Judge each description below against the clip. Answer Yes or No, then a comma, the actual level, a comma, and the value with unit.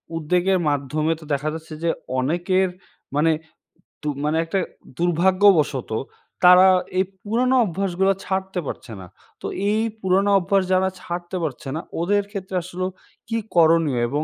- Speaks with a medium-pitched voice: Yes, medium, 180 Hz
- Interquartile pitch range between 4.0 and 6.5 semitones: No, average, 3.2 semitones